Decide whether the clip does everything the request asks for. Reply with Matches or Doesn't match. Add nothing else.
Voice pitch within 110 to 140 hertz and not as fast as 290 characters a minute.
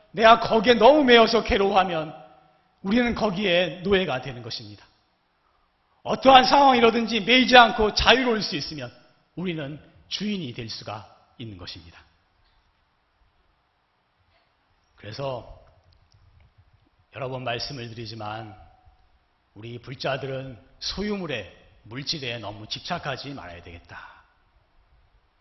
Matches